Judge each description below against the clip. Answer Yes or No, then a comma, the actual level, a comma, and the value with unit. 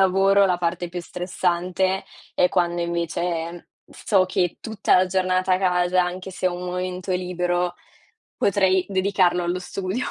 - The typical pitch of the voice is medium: Yes, medium, 180 Hz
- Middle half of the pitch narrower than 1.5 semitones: Yes, narrow, 1.0 semitones